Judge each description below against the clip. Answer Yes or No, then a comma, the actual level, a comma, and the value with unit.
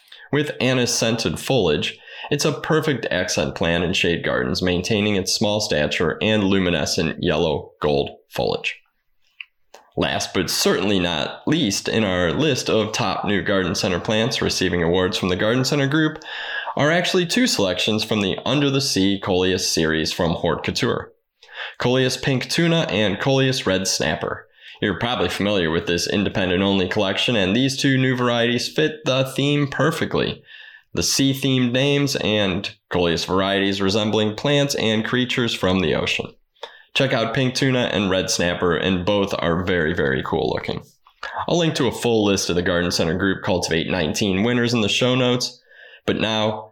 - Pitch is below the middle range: Yes, low, 110 Hz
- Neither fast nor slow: Yes, average, 165 wpm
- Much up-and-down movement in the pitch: Yes, wide, 6.0 semitones